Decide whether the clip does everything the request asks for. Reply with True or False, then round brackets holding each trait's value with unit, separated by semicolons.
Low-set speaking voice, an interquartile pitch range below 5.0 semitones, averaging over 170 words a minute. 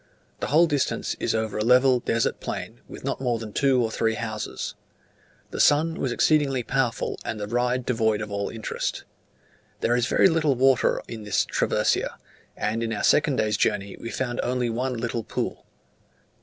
True (120 Hz; 3.0 semitones; 180 wpm)